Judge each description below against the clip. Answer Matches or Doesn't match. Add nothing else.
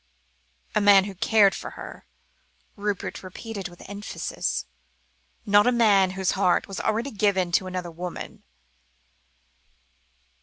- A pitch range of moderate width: Doesn't match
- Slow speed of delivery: Matches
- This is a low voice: Doesn't match